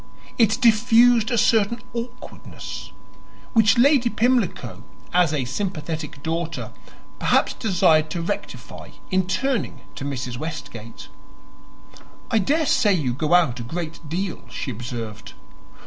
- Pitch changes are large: Yes, wide, 7.4 semitones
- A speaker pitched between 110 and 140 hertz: No, medium, 180 Hz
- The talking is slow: Yes, slow, 115 wpm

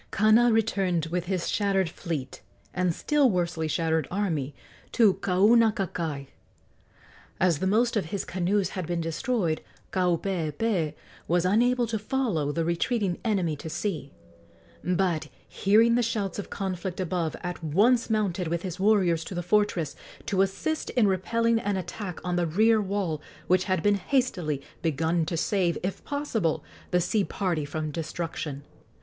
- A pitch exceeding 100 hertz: Yes, medium, 185 Hz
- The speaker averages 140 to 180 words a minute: Yes, average, 150 wpm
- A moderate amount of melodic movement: Yes, average, 4.0 semitones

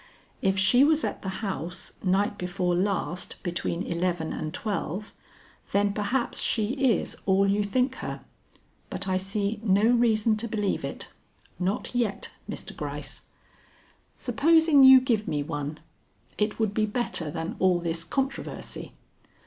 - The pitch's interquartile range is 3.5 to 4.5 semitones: Yes, average, 4.2 semitones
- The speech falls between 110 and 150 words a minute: Yes, average, 140 wpm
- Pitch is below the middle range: No, high, 200 Hz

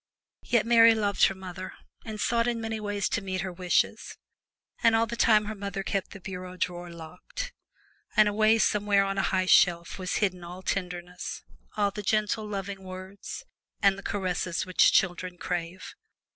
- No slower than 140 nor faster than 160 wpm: No, average, 170 wpm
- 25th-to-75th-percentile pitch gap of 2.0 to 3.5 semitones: Yes, average, 2.7 semitones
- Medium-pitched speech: No, high, 195 Hz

